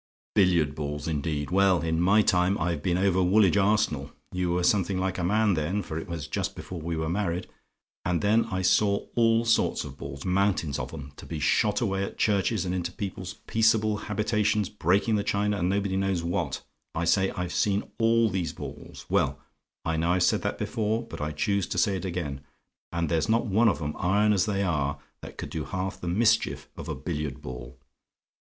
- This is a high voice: No, very low, 95 Hz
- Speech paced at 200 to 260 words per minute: Yes, fast, 205 wpm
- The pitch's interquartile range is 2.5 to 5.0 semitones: Yes, average, 3.7 semitones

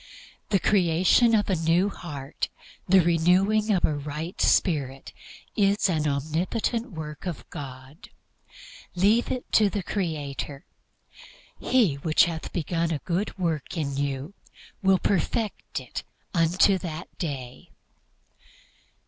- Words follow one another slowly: Yes, slow, 120 wpm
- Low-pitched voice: No, medium, 170 Hz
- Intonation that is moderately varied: Yes, average, 4.5 semitones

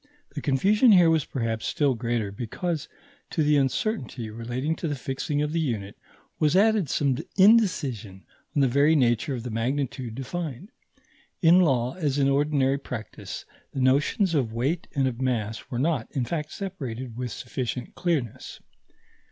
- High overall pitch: No, low, 135 Hz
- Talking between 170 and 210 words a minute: No, average, 160 wpm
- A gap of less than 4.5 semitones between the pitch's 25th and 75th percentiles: No, average, 4.8 semitones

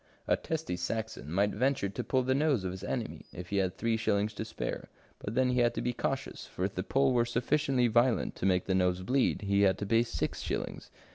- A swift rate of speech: Yes, fast, 235 wpm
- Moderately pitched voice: No, low, 115 Hz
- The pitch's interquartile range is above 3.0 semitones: Yes, average, 4.7 semitones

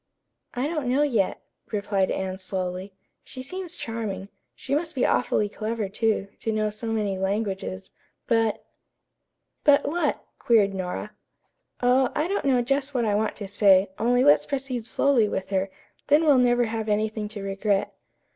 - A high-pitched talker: Yes, high, 220 Hz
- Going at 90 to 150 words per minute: No, average, 165 wpm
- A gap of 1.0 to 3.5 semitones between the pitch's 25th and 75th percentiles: No, average, 4.5 semitones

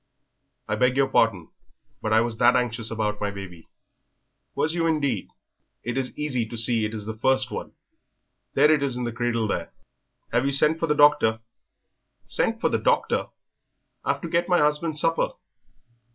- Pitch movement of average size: Yes, average, 5.0 semitones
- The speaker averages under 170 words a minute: No, average, 180 wpm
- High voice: No, low, 125 Hz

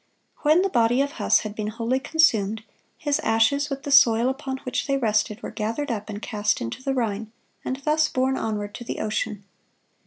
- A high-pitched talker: Yes, high, 235 Hz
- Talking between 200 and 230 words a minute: Yes, fast, 205 wpm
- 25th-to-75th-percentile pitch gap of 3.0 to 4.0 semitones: No, average, 4.4 semitones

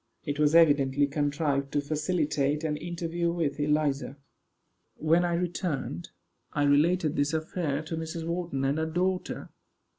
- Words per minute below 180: Yes, average, 140 wpm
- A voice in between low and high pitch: Yes, medium, 155 Hz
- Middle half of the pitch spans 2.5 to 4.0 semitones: Yes, average, 2.8 semitones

